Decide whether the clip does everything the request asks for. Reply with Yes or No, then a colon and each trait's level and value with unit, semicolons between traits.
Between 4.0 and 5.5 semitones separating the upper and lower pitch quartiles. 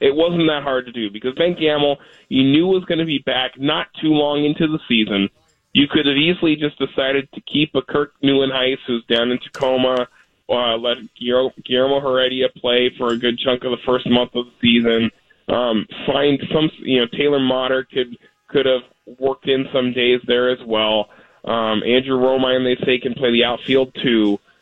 No: average, 2.7 semitones